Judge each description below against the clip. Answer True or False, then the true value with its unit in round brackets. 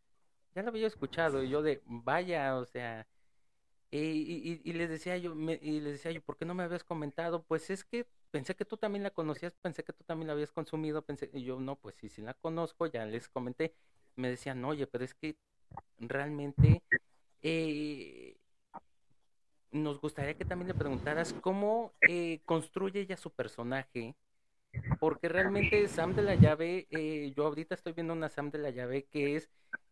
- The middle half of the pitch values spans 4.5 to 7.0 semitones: False (3.9 semitones)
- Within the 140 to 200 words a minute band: True (185 wpm)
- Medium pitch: True (155 Hz)